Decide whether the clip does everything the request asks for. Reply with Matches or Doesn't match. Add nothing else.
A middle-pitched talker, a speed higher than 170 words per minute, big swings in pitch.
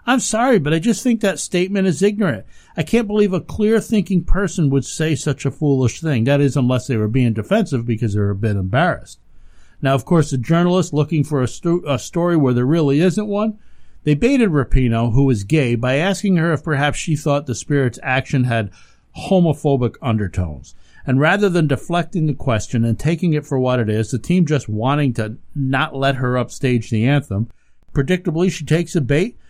Matches